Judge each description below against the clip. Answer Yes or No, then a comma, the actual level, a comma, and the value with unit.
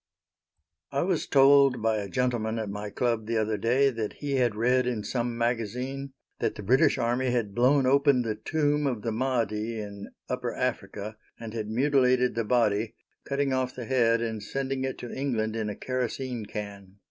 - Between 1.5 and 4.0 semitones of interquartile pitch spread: Yes, average, 3.3 semitones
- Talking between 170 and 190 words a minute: Yes, average, 180 wpm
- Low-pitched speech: Yes, low, 120 Hz